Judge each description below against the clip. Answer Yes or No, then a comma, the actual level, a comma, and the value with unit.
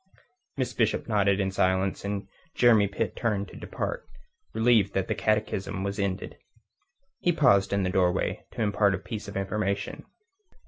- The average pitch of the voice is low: Yes, low, 100 Hz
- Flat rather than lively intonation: Yes, narrow, 2.0 semitones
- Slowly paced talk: No, average, 155 wpm